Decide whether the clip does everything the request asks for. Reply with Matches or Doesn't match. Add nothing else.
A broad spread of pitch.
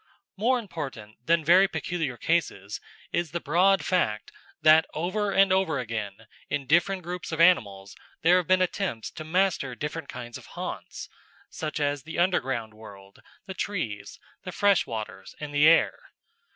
Matches